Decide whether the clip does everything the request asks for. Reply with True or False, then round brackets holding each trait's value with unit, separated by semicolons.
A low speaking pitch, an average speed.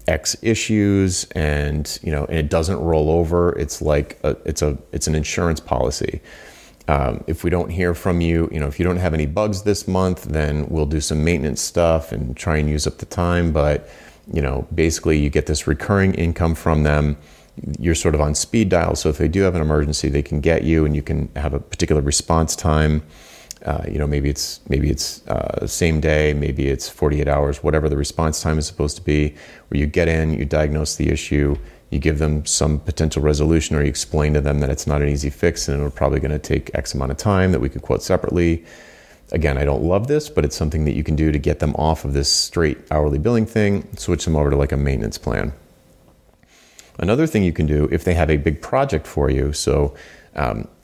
False (75 Hz; 230 wpm)